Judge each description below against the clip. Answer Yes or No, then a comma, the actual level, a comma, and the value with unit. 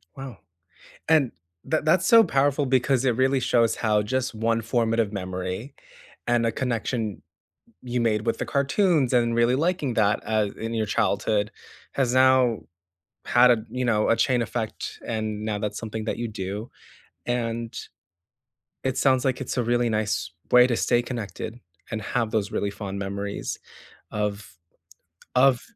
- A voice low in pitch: Yes, low, 115 Hz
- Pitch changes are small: No, average, 3.1 semitones